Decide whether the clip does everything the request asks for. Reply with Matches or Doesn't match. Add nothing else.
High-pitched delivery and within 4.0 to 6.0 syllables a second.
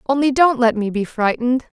Matches